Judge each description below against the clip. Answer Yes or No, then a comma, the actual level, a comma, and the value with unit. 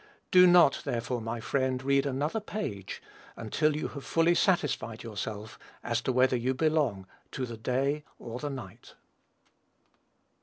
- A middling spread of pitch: Yes, average, 4.5 semitones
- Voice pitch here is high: No, low, 130 Hz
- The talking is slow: No, average, 145 wpm